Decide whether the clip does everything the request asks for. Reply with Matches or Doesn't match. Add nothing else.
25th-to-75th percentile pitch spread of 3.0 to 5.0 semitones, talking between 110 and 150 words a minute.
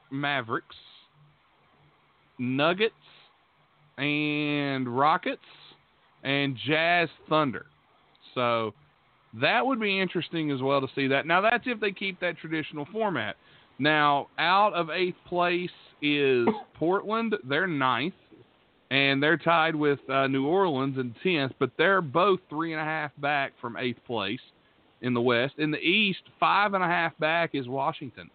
Matches